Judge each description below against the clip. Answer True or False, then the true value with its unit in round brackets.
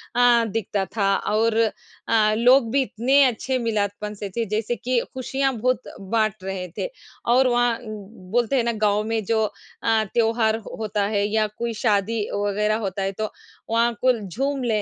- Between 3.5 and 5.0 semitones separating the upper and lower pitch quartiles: False (2.4 semitones)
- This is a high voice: True (225 Hz)